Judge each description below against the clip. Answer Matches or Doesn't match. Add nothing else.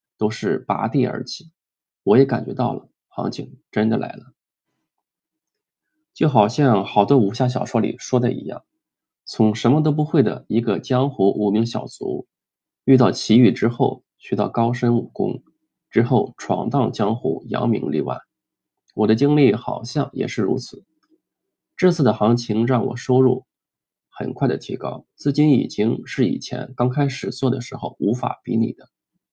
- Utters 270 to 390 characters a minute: Doesn't match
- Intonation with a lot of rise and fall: Doesn't match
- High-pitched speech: Doesn't match